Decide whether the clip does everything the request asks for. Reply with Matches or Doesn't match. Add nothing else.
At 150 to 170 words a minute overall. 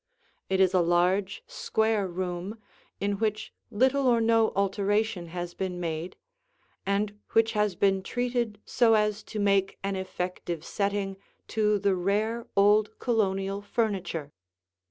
Doesn't match